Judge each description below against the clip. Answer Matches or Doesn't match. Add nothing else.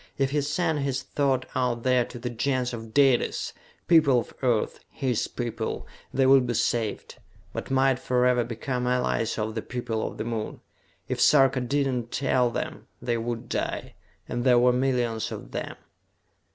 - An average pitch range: Doesn't match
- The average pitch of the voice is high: Doesn't match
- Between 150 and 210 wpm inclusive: Matches